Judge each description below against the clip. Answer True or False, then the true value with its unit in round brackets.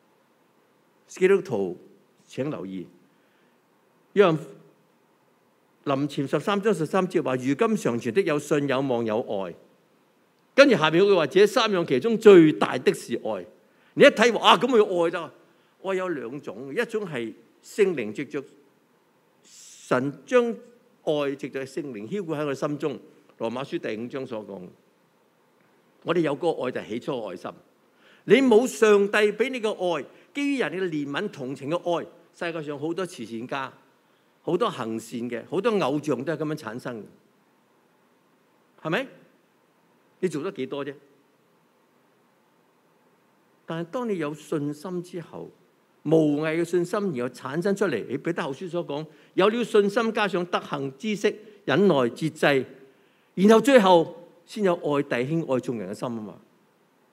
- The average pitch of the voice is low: False (165 Hz)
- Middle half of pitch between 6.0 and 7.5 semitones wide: True (6.7 semitones)